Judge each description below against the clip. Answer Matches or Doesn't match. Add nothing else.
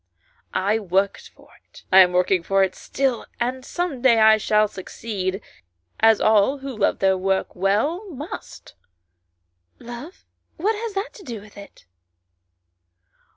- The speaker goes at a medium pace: Matches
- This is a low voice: Doesn't match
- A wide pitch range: Matches